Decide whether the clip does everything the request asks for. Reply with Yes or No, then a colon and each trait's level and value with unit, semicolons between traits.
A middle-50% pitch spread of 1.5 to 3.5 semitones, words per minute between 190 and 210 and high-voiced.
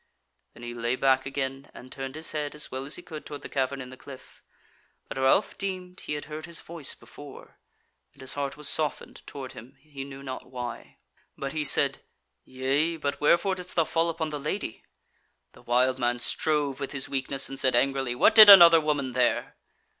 No: average, 2.9 semitones; average, 200 wpm; medium, 140 Hz